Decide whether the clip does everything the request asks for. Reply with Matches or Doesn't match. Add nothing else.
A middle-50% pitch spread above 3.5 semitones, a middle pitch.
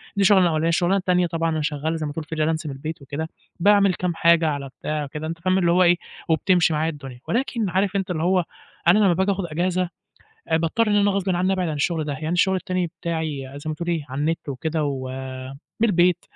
Doesn't match